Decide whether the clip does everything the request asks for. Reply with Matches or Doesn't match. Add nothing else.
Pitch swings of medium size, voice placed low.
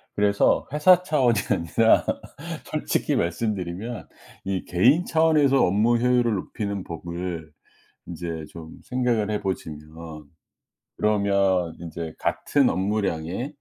Doesn't match